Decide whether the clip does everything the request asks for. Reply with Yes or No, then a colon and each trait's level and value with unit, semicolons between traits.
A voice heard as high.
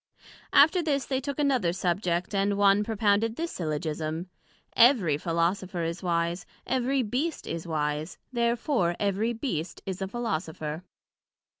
Yes: high, 195 Hz